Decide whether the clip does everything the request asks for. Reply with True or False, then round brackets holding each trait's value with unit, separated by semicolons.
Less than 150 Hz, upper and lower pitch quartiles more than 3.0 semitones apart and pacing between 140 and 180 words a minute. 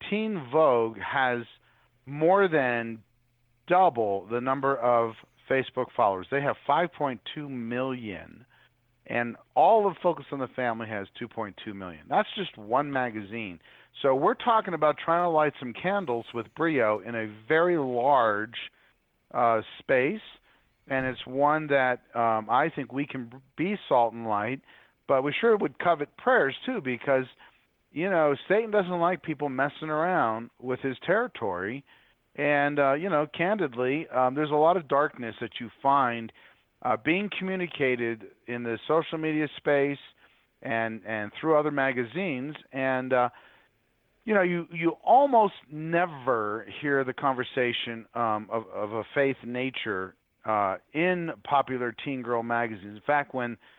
True (135 Hz; 4.8 semitones; 145 wpm)